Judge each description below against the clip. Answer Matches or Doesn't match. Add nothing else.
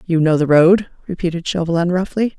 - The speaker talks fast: Doesn't match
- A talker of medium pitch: Matches